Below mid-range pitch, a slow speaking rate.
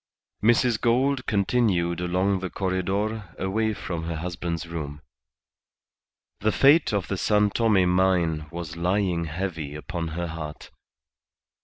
Yes: very low, 90 Hz; slow, 125 wpm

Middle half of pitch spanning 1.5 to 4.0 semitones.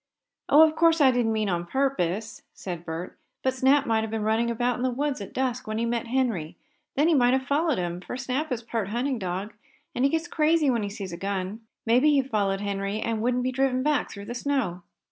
No: average, 4.8 semitones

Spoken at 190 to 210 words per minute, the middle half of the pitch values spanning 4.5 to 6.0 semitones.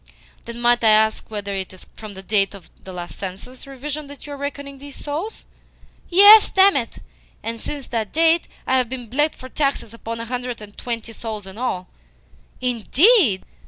Yes: average, 195 wpm; average, 4.8 semitones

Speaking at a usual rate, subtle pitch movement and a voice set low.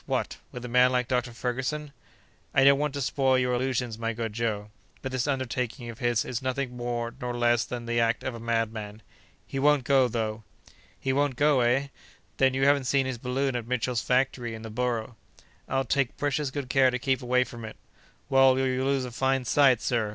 No: fast, 210 wpm; narrow, 2.1 semitones; low, 125 Hz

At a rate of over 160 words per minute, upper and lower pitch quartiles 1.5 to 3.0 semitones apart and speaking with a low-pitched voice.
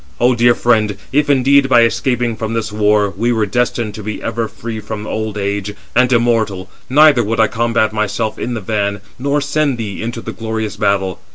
Yes: average, 195 wpm; narrow, 2.4 semitones; low, 115 Hz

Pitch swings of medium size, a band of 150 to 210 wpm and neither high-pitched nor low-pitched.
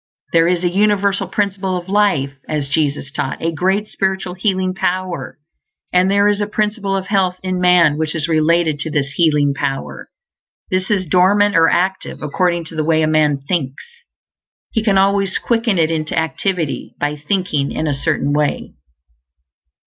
Yes: average, 3.9 semitones; average, 170 wpm; medium, 180 Hz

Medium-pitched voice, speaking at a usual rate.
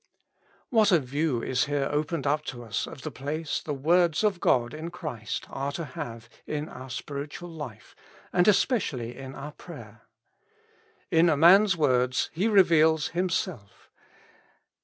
Yes: medium, 150 Hz; average, 150 wpm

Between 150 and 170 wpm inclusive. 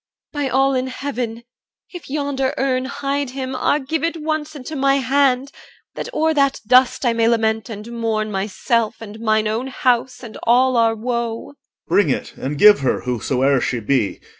No: average, 180 wpm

